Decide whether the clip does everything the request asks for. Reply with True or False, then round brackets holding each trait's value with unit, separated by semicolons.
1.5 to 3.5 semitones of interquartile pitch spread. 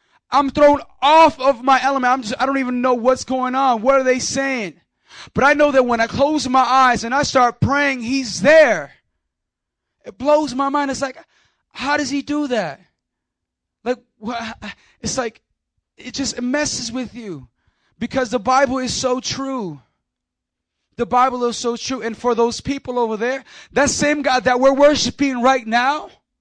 True (2.5 semitones)